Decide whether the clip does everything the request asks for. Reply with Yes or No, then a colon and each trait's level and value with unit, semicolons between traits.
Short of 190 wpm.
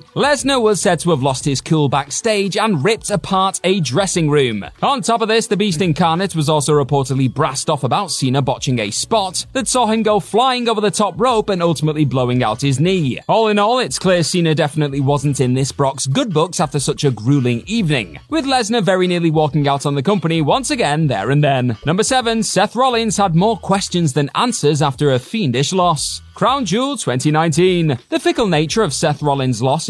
No: fast, 205 wpm